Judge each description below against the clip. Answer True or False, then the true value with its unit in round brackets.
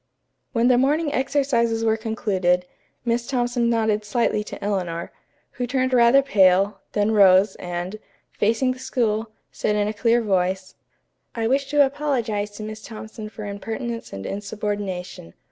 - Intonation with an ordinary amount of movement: True (3.1 semitones)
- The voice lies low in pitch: False (220 Hz)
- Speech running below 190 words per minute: True (145 wpm)